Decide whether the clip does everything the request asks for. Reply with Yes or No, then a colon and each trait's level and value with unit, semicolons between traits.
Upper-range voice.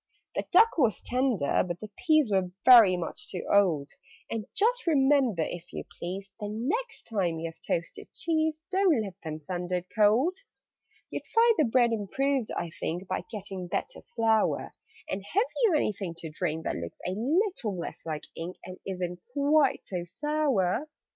Yes: high, 210 Hz